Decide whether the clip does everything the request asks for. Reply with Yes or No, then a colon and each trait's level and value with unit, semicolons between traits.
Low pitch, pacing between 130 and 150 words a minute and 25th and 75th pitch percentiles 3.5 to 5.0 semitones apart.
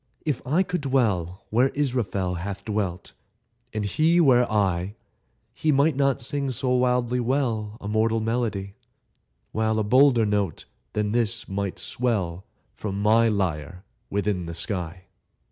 Yes: low, 110 Hz; average, 140 wpm; average, 4.2 semitones